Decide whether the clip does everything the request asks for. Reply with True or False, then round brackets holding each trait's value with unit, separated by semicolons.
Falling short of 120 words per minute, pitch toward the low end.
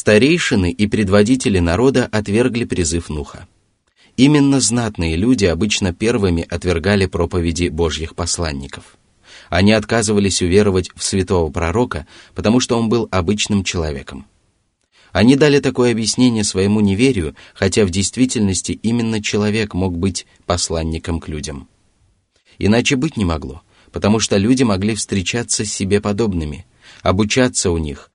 False (125 wpm; 100 Hz)